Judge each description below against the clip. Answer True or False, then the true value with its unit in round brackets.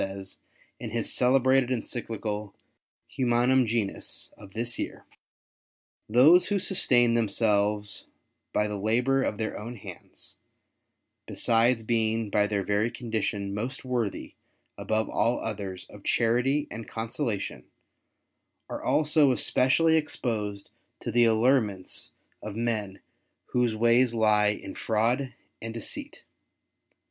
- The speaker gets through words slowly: True (115 wpm)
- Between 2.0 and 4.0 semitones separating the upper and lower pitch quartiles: True (2.9 semitones)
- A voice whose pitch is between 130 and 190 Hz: False (115 Hz)